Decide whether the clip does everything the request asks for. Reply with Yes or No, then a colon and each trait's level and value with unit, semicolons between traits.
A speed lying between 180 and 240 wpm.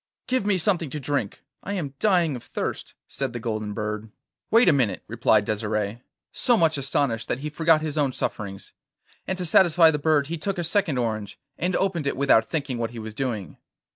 Yes: average, 200 wpm